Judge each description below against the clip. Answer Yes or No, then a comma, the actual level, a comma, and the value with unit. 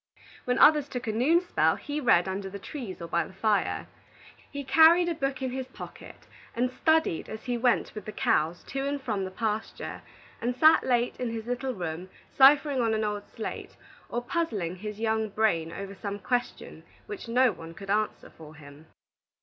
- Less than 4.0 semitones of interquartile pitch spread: No, average, 5.1 semitones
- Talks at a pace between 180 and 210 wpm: Yes, average, 190 wpm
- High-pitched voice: Yes, high, 230 Hz